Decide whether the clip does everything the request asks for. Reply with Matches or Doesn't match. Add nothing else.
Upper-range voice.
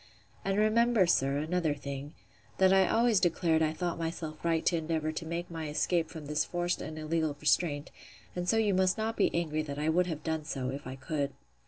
Doesn't match